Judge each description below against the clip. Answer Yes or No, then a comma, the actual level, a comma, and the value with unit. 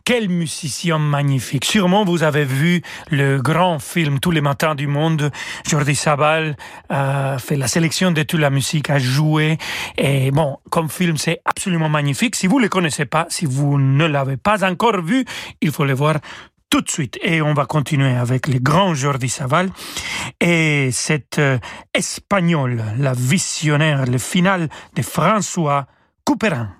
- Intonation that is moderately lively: Yes, average, 3.7 semitones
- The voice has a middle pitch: Yes, medium, 155 Hz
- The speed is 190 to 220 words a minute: No, average, 170 wpm